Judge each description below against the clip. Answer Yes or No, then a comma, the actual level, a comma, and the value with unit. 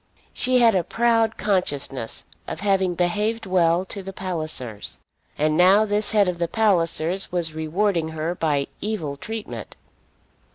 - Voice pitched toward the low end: No, medium, 180 Hz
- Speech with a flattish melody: No, average, 4.6 semitones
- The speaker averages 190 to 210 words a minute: No, average, 140 wpm